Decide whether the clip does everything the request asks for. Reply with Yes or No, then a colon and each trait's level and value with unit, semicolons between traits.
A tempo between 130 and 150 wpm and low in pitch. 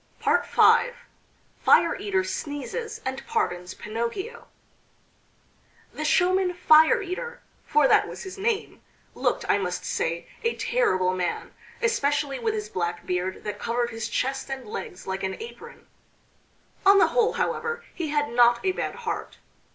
No: average, 145 wpm; very high, 290 Hz